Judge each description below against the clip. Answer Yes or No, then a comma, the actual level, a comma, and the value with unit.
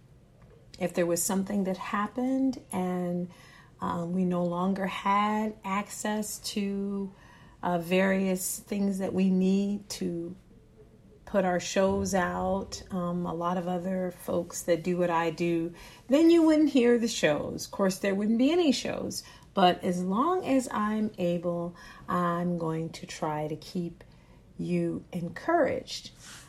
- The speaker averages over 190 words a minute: No, average, 145 wpm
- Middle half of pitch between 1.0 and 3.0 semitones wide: Yes, average, 2.7 semitones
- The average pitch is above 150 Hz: Yes, medium, 185 Hz